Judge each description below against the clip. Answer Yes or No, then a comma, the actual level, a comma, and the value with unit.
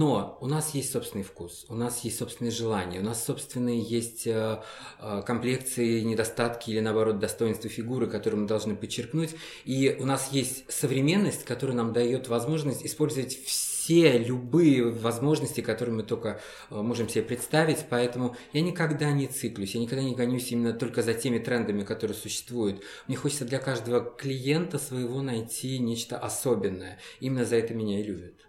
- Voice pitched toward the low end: Yes, low, 120 Hz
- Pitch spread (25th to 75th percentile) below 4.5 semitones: Yes, average, 2.9 semitones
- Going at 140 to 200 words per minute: Yes, fast, 160 wpm